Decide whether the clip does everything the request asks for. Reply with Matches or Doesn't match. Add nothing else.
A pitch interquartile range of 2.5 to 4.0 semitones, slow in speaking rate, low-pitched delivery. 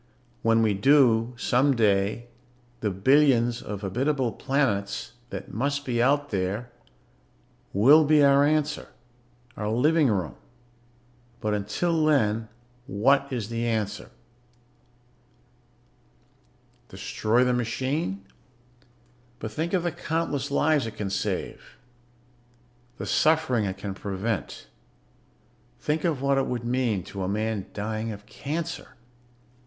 Doesn't match